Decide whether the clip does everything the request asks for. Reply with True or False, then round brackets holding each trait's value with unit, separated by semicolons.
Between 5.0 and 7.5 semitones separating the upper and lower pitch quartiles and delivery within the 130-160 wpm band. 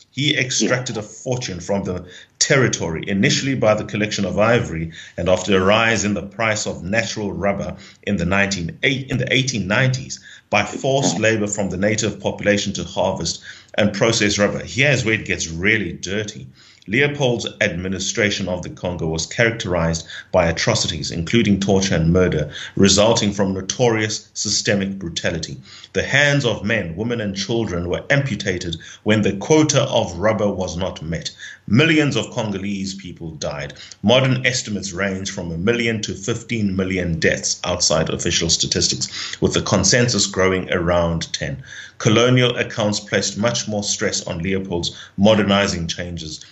False (3.8 semitones; 150 wpm)